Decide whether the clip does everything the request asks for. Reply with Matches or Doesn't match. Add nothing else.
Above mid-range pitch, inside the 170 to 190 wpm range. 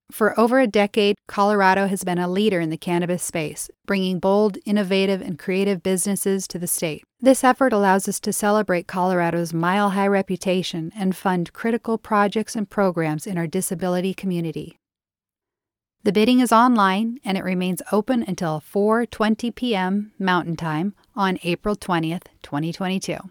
Doesn't match